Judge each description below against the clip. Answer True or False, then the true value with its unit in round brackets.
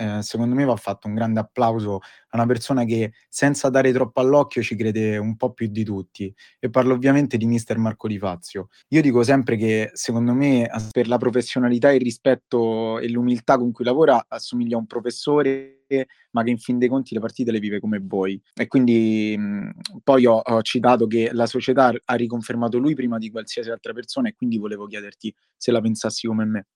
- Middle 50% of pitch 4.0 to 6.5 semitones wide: False (2.7 semitones)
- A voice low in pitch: True (120 Hz)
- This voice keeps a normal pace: False (200 wpm)